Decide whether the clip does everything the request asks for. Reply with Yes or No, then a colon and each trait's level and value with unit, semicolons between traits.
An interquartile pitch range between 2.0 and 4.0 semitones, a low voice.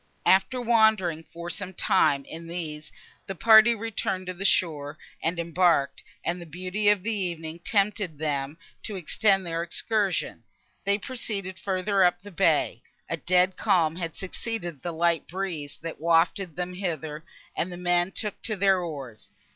No: average, 3.2 semitones; medium, 180 Hz